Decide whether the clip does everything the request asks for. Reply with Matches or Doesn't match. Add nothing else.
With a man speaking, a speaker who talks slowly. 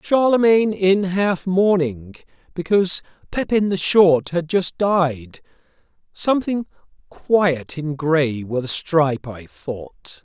Matches